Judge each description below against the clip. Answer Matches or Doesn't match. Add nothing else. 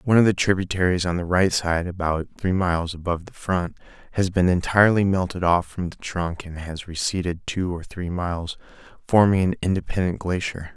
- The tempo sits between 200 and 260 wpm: Doesn't match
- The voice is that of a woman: Doesn't match